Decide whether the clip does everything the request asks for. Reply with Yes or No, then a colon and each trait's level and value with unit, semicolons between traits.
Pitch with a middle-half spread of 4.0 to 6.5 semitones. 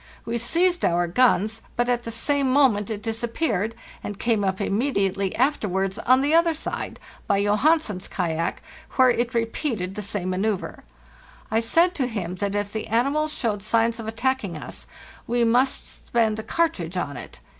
Yes: average, 4.3 semitones